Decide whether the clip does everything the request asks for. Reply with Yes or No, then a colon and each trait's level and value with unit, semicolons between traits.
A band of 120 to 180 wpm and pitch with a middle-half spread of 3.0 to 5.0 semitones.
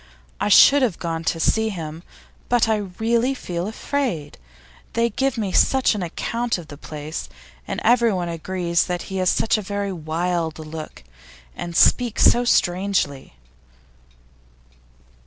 No: average, 140 wpm; wide, 5.5 semitones